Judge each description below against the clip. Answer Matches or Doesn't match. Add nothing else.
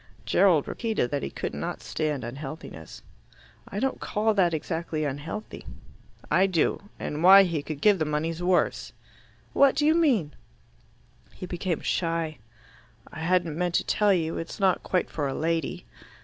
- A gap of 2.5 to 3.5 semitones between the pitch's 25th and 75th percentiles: Doesn't match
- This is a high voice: Doesn't match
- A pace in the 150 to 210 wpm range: Matches